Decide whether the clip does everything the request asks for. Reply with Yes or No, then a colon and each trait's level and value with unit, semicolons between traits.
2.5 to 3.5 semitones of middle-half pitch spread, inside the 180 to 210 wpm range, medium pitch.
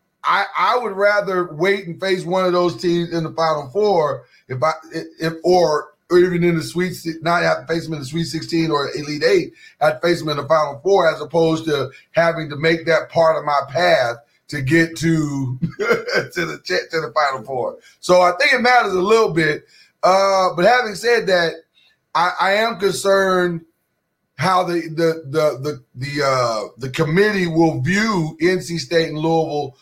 Yes: average, 2.9 semitones; average, 195 wpm; medium, 165 Hz